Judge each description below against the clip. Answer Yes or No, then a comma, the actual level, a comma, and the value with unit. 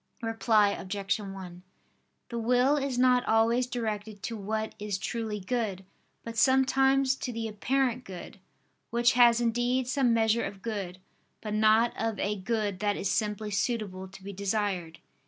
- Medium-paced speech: Yes, average, 155 wpm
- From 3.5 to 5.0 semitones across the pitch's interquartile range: No, average, 3.1 semitones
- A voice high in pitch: Yes, high, 220 Hz